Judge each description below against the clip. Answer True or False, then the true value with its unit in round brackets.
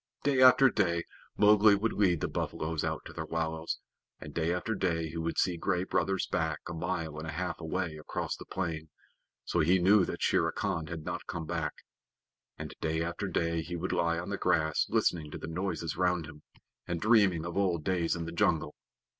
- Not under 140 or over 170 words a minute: False (205 wpm)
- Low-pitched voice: True (85 Hz)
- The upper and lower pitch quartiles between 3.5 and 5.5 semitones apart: False (2.6 semitones)